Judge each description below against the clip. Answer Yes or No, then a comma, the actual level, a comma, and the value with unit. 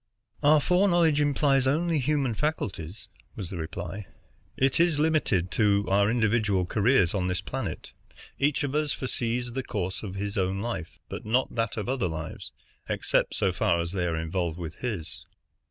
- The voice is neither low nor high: No, low, 110 Hz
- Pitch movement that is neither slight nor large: No, wide, 7.0 semitones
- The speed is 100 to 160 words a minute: No, average, 170 wpm